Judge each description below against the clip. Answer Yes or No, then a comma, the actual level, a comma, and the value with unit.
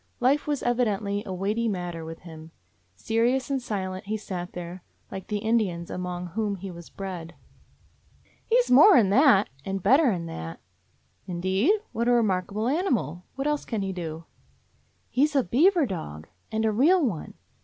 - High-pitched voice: Yes, high, 205 Hz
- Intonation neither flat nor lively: No, wide, 5.7 semitones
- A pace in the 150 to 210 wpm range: Yes, average, 175 wpm